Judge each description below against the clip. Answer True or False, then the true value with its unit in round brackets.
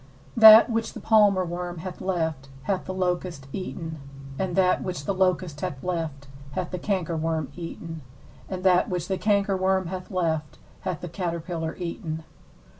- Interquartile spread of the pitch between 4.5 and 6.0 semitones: False (2.5 semitones)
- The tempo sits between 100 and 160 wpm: True (150 wpm)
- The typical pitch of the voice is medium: True (180 Hz)